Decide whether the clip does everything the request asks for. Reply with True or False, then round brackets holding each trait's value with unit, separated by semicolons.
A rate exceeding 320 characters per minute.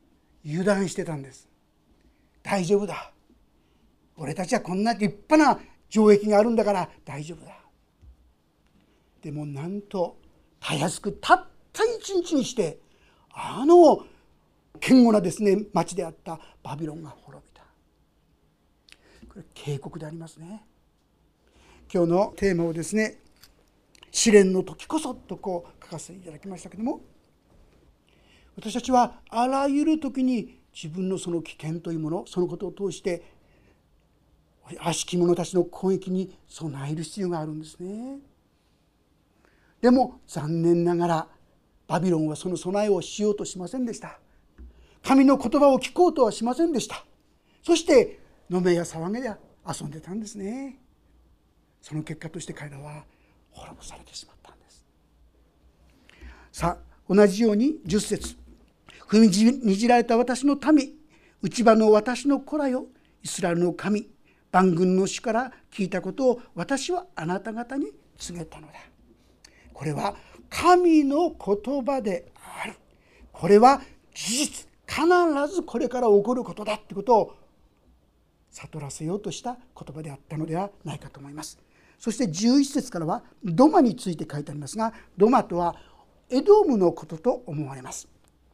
False (275 characters per minute)